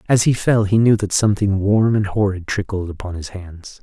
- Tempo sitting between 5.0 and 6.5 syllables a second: Yes, 5.2 syllables/s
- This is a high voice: No, low, 100 Hz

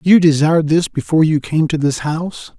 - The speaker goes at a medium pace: No, fast, 210 wpm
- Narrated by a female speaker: No, male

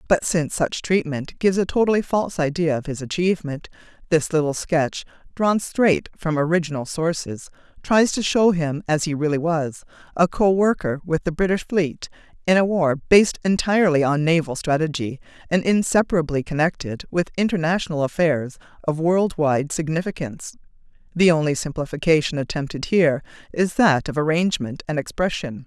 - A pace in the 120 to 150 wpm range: Yes, average, 145 wpm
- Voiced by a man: No, female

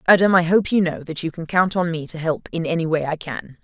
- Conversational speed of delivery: No, fast, 295 wpm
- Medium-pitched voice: Yes, medium, 170 Hz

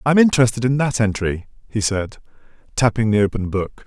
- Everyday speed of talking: Yes, average, 170 wpm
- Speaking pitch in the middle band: No, low, 115 Hz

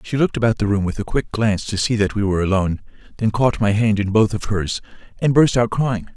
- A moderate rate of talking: No, fast, 265 wpm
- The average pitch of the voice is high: No, low, 105 Hz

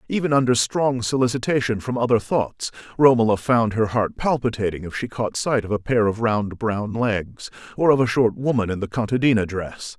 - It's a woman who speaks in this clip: No, male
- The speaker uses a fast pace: No, average, 190 wpm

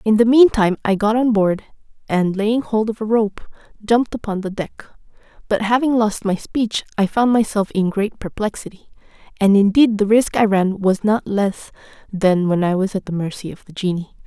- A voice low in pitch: No, high, 210 Hz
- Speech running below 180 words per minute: No, average, 200 wpm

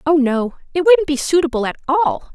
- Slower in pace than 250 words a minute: Yes, fast, 205 wpm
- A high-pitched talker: Yes, very high, 310 Hz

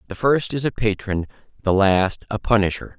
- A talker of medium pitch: No, low, 105 Hz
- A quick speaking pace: No, average, 180 wpm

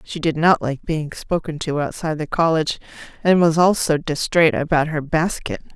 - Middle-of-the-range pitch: Yes, medium, 160 Hz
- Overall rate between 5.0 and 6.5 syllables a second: Yes, 5.1 syllables/s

